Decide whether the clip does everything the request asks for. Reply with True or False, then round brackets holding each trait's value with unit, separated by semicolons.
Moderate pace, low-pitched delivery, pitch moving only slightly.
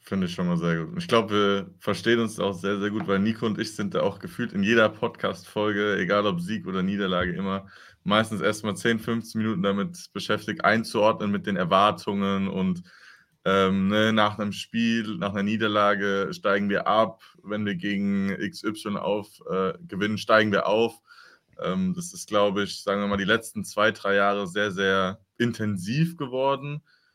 True (180 wpm; 100 Hz; 2.1 semitones)